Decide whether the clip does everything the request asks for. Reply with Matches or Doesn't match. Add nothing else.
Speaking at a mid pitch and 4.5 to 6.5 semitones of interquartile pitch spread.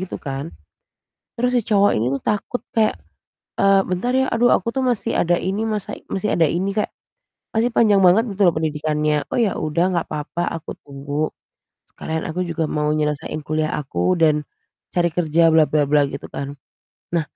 Matches